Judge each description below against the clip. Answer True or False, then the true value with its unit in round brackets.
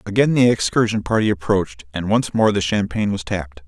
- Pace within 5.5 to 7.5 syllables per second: True (6.0 syllables/s)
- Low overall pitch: True (100 Hz)